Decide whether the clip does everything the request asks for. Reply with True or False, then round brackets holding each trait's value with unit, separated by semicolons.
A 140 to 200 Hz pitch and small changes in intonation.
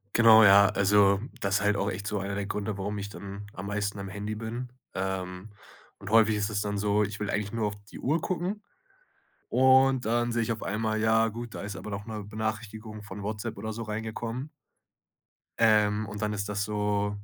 False (105 Hz; 1.7 semitones)